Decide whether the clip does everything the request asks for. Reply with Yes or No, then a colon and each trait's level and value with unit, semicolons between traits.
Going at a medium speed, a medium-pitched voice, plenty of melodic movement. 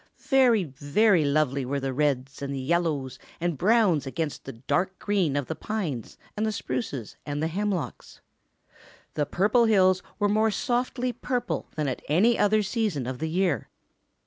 Yes: average, 160 wpm; medium, 170 Hz; wide, 6.9 semitones